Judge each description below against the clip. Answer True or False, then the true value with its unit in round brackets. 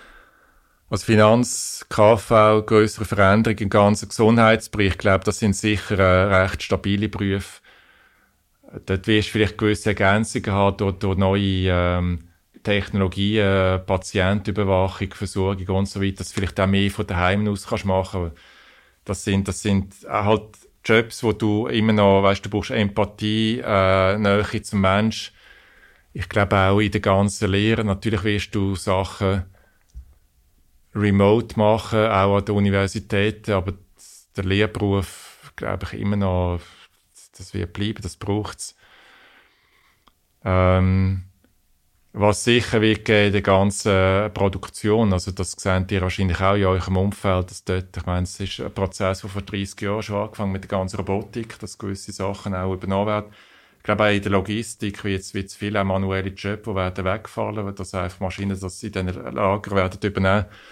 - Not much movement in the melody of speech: True (1.8 semitones)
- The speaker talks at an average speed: True (160 wpm)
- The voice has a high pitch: False (100 Hz)